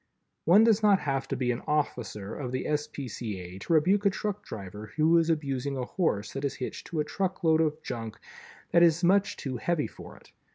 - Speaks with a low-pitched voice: No, medium, 150 Hz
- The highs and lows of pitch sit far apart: Yes, wide, 5.7 semitones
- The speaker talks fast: Yes, fast, 220 wpm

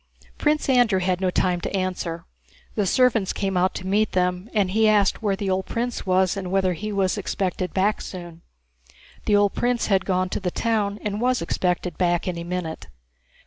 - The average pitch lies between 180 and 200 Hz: Yes, high, 190 Hz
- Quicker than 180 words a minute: Yes, average, 190 wpm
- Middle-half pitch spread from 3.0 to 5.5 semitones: No, narrow, 2.6 semitones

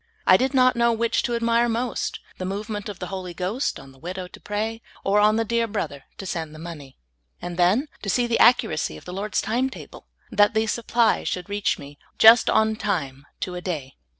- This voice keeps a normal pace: No, fast, 220 wpm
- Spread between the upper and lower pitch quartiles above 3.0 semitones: Yes, average, 4.4 semitones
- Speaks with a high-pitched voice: Yes, high, 205 Hz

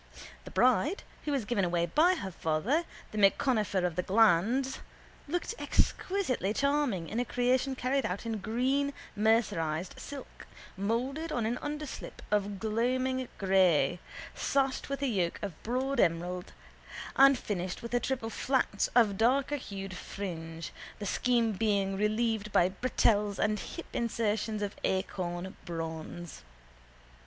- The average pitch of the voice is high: Yes, high, 220 Hz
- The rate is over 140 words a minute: No, slow, 135 wpm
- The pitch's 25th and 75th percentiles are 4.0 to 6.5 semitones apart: Yes, wide, 5.4 semitones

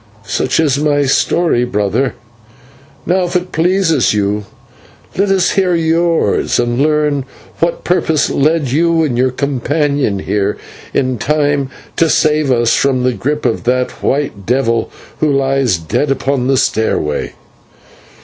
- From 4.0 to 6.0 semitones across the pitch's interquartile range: Yes, average, 4.5 semitones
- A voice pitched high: No, medium, 140 Hz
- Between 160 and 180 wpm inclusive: No, average, 140 wpm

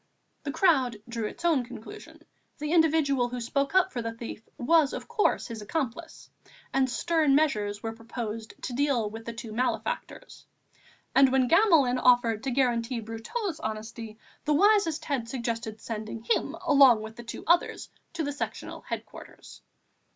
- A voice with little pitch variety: No, average, 5.0 semitones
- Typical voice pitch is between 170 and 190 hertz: No, very high, 250 Hz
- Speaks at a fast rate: No, average, 160 wpm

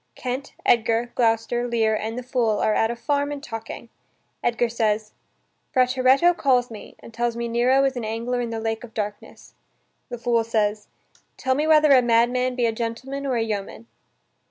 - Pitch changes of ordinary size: No, narrow, 2.1 semitones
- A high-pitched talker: Yes, high, 235 Hz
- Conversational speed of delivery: Yes, average, 180 wpm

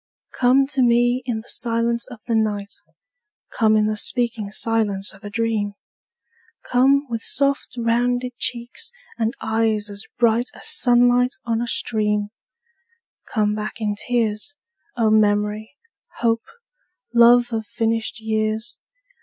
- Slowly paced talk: Yes, slow, 130 wpm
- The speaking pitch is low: No, high, 225 Hz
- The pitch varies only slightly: Yes, narrow, 2.1 semitones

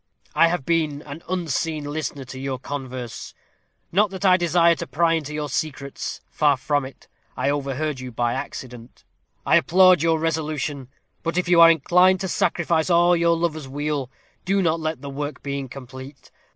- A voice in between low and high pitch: Yes, medium, 155 Hz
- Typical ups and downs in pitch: Yes, average, 3.5 semitones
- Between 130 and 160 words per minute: No, average, 180 wpm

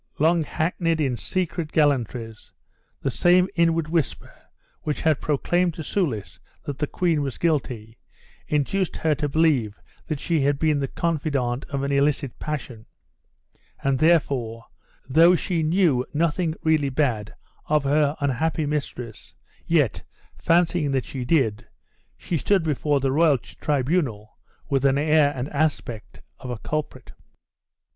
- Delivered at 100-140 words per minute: Yes, slow, 135 wpm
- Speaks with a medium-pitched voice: Yes, medium, 150 Hz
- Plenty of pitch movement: No, average, 3.5 semitones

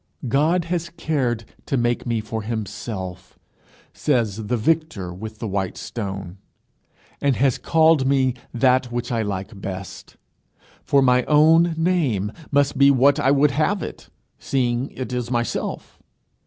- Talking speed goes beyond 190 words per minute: No, average, 140 wpm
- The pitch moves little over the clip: No, average, 4.6 semitones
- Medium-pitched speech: No, low, 125 Hz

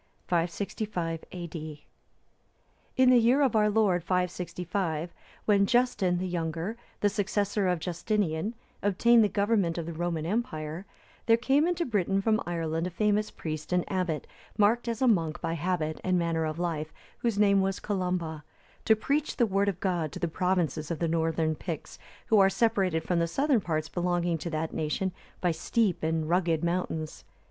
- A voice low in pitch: No, medium, 180 Hz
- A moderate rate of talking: Yes, average, 170 wpm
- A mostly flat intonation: No, average, 4.2 semitones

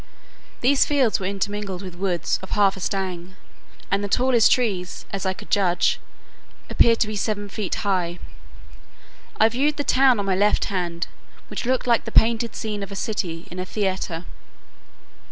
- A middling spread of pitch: Yes, average, 3.3 semitones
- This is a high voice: Yes, high, 200 Hz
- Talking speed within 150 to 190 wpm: Yes, average, 170 wpm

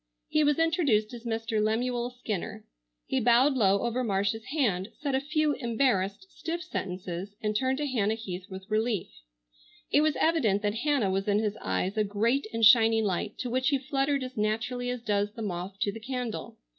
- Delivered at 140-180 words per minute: No, average, 190 wpm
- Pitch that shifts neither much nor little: Yes, average, 4.2 semitones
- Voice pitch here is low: No, high, 225 Hz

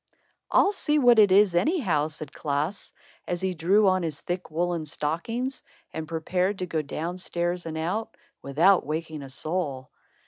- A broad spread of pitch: No, average, 3.6 semitones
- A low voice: No, medium, 175 Hz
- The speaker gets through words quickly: No, average, 165 wpm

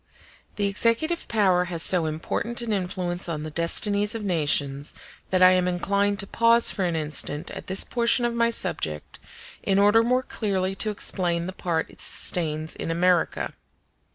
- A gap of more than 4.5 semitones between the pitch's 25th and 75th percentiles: No, average, 4.1 semitones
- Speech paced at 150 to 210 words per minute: Yes, average, 170 wpm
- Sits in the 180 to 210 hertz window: Yes, medium, 185 Hz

